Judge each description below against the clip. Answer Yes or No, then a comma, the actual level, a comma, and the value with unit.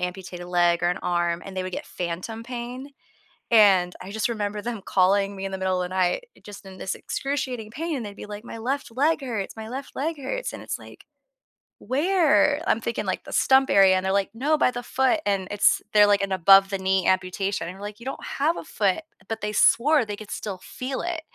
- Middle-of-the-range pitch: No, high, 205 Hz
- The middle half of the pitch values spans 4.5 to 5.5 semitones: Yes, average, 5.2 semitones